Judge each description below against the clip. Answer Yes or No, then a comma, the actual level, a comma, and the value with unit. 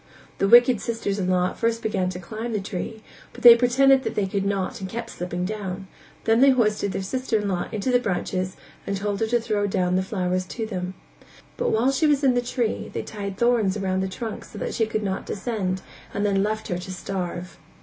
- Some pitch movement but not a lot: Yes, average, 3.6 semitones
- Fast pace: Yes, fast, 230 wpm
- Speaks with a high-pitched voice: Yes, high, 205 Hz